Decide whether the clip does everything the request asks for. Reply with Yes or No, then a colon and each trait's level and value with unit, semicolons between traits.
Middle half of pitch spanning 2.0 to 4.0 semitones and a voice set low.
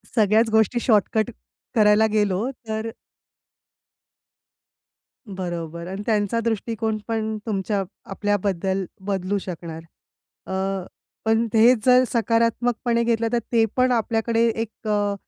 No: average, 2.8 semitones; high, 220 Hz